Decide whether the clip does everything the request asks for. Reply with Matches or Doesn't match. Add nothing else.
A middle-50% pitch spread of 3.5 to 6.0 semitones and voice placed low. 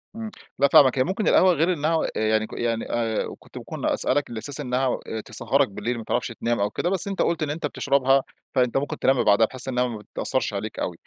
Matches